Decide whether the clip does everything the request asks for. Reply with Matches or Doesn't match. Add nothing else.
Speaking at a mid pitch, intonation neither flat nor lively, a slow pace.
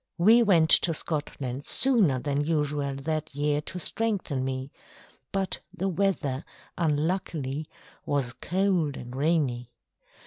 Matches